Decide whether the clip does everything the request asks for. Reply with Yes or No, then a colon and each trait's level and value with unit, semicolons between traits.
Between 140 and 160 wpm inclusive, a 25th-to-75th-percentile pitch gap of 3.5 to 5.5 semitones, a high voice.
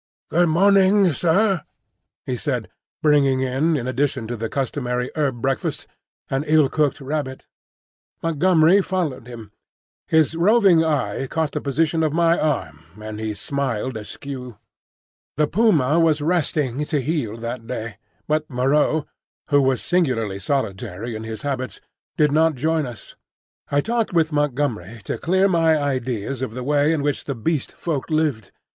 No: average, 150 wpm; average, 4.4 semitones; medium, 145 Hz